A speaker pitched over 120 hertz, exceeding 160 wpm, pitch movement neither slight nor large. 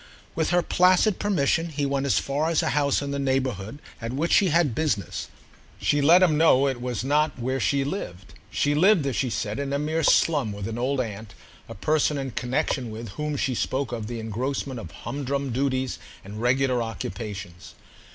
Yes: low, 135 Hz; average, 195 wpm; average, 4.2 semitones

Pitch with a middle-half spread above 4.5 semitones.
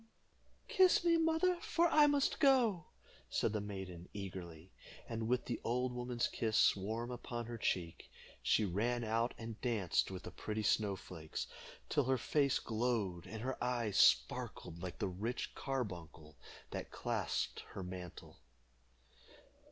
Yes: average, 5.1 semitones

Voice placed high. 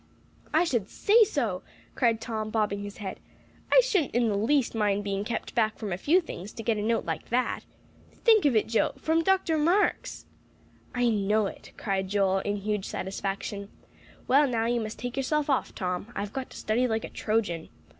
Yes: high, 225 Hz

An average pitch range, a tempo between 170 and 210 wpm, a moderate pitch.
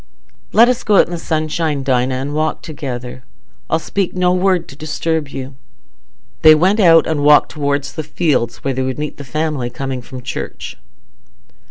Yes: average, 3.5 semitones; average, 180 wpm; medium, 150 Hz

